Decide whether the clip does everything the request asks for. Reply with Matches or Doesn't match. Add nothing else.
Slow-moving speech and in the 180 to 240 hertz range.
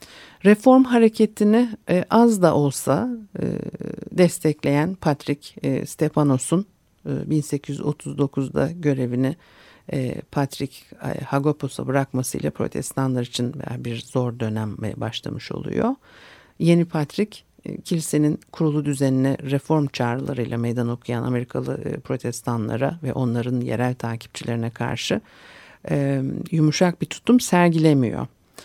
Doesn't match